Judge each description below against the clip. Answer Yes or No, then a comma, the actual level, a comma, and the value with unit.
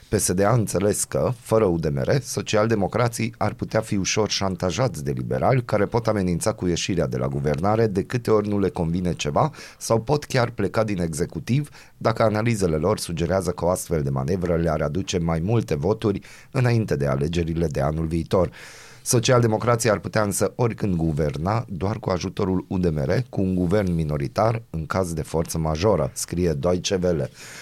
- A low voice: Yes, very low, 95 Hz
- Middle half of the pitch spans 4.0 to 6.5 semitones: Yes, average, 4.7 semitones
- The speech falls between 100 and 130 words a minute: No, average, 165 wpm